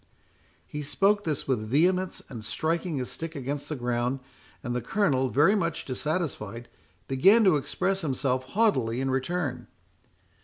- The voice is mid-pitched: Yes, medium, 145 Hz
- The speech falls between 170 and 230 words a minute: No, average, 145 wpm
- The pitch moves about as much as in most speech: No, wide, 5.7 semitones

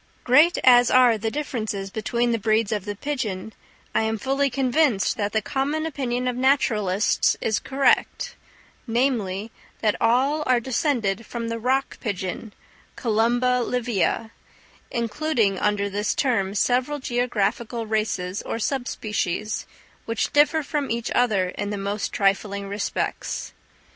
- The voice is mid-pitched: No, high, 230 Hz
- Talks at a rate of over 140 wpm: No, slow, 135 wpm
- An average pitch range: Yes, average, 3.7 semitones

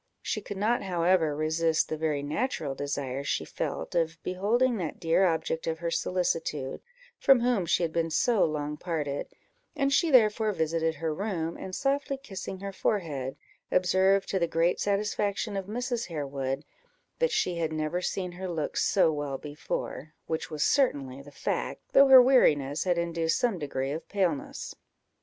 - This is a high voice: No, medium, 170 Hz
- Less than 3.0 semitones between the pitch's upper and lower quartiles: No, average, 4.8 semitones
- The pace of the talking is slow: No, average, 165 wpm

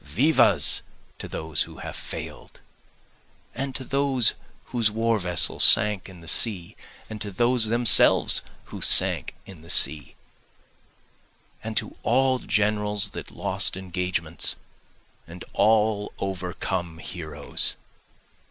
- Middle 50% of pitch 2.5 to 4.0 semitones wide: No, average, 4.7 semitones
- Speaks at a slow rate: Yes, slow, 115 wpm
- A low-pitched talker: Yes, low, 105 Hz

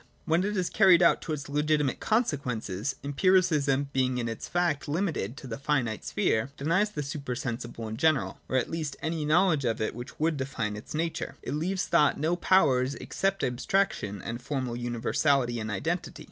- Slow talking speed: No, average, 190 wpm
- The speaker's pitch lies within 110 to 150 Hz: Yes, medium, 140 Hz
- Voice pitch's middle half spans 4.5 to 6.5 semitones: Yes, average, 5.2 semitones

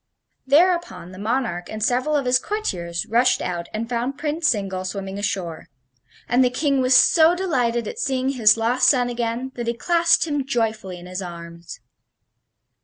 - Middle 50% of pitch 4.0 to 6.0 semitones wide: Yes, wide, 5.6 semitones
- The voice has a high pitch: Yes, high, 240 Hz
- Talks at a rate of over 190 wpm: No, average, 170 wpm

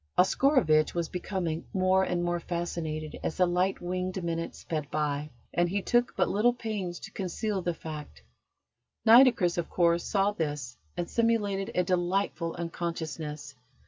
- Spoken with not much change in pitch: No, average, 3.1 semitones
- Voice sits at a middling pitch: Yes, medium, 175 Hz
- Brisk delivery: No, average, 145 wpm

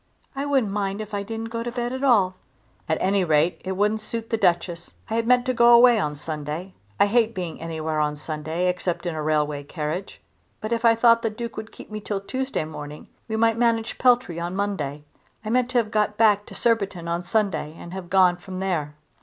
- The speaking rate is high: Yes, fast, 220 wpm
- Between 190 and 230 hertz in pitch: Yes, high, 200 Hz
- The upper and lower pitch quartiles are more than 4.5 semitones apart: Yes, average, 5.2 semitones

